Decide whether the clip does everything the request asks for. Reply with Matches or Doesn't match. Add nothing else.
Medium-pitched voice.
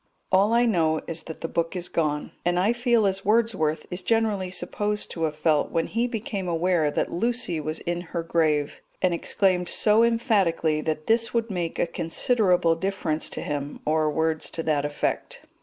Matches